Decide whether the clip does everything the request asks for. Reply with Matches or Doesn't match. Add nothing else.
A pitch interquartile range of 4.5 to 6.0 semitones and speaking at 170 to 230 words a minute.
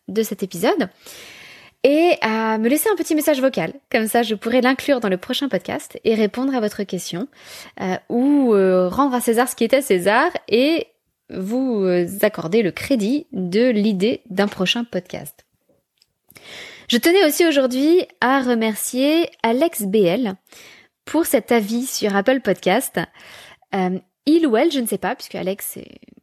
Doesn't match